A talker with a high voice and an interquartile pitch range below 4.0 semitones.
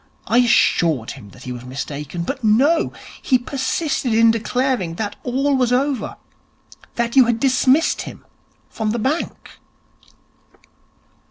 No: high, 240 Hz; average, 4.5 semitones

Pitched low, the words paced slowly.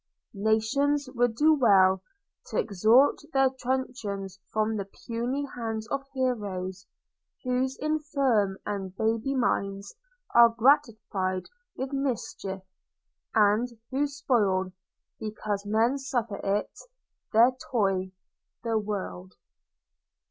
No: high, 225 Hz; slow, 100 wpm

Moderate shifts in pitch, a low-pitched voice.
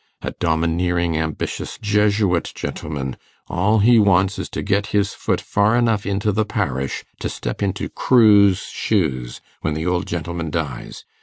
Yes: average, 4.2 semitones; very low, 95 Hz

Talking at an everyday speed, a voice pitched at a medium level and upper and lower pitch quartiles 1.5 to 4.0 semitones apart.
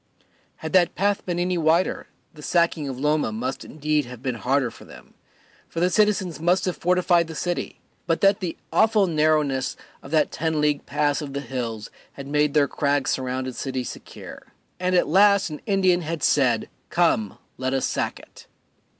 No: average, 180 wpm; medium, 155 Hz; average, 4.6 semitones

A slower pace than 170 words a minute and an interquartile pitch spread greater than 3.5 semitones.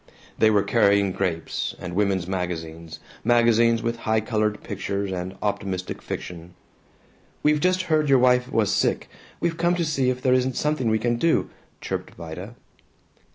Yes: average, 155 wpm; average, 5.2 semitones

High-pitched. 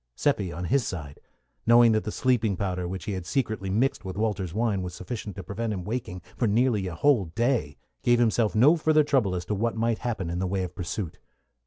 No: low, 105 Hz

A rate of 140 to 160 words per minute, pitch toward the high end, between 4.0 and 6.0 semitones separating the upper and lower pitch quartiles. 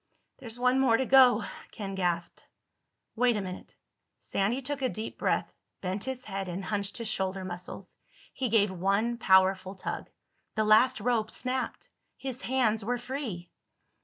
Yes: average, 155 wpm; high, 215 Hz; average, 4.5 semitones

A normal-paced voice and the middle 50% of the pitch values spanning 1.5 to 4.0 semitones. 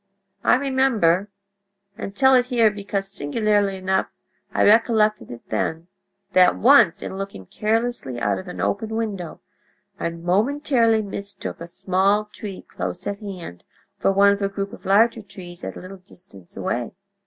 Yes: average, 150 wpm; average, 2.9 semitones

